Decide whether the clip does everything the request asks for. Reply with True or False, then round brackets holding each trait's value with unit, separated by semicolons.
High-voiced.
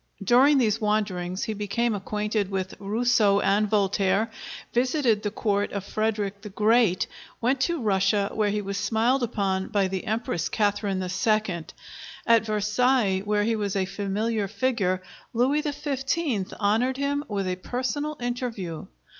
True (210 Hz)